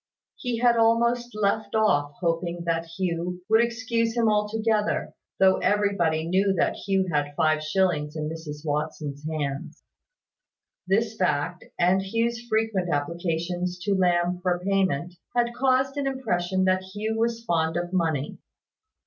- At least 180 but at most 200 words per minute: No, average, 140 wpm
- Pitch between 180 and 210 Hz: Yes, medium, 185 Hz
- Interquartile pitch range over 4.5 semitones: Yes, average, 5.1 semitones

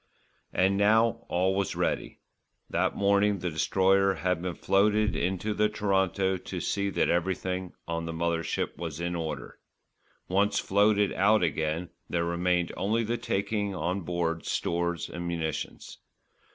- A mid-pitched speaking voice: No, very low, 95 Hz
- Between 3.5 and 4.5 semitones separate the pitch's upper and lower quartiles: No, average, 2.8 semitones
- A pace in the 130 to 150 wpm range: Yes, average, 145 wpm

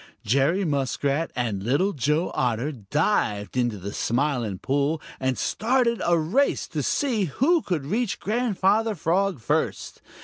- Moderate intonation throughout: No, wide, 8.0 semitones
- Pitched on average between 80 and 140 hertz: No, medium, 150 Hz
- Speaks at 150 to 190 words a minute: No, slow, 135 wpm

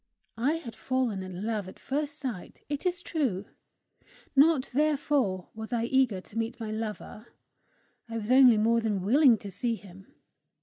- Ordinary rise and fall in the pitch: Yes, average, 4.4 semitones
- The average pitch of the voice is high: Yes, high, 230 Hz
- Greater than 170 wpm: No, average, 165 wpm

